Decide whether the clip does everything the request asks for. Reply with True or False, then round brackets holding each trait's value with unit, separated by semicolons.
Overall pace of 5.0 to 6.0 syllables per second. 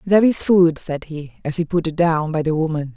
True (5.5 syllables/s)